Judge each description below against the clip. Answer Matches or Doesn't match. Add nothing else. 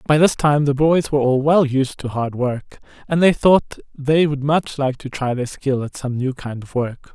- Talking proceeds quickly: Matches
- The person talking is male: Matches